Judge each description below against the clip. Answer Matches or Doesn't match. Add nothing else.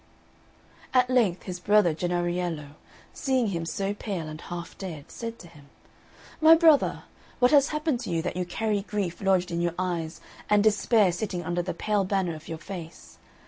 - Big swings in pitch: Doesn't match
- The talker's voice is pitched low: Doesn't match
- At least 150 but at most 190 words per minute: Matches